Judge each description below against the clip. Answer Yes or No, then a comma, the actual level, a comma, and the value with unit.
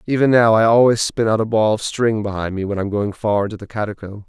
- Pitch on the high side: No, low, 110 Hz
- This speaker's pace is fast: Yes, fast, 280 wpm